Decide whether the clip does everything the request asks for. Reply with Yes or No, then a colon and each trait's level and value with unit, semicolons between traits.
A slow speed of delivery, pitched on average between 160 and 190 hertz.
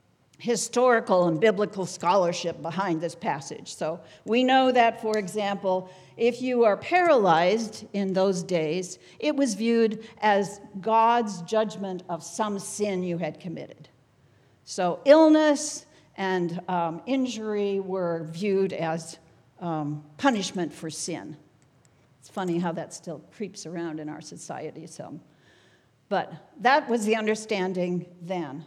Yes: slow, 130 wpm; medium, 185 Hz